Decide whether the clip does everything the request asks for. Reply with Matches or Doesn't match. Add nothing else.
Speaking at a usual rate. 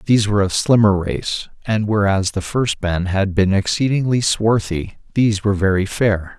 Matches